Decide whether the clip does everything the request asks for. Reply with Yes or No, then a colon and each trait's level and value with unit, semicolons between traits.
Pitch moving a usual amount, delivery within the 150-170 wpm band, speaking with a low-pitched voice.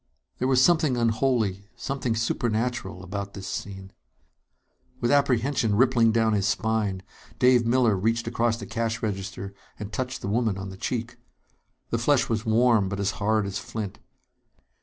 Yes: average, 3.3 semitones; average, 155 wpm; low, 110 Hz